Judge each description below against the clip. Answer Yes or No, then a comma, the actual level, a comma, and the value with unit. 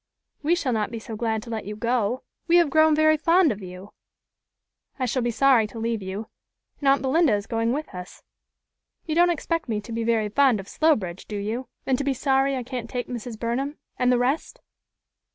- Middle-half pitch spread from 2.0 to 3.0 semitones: No, average, 4.3 semitones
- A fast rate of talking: Yes, fast, 215 wpm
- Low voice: No, high, 245 Hz